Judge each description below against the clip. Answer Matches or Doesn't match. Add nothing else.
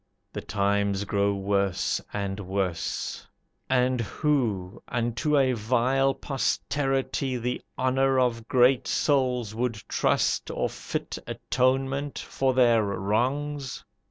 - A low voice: Matches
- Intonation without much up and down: Doesn't match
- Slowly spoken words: Matches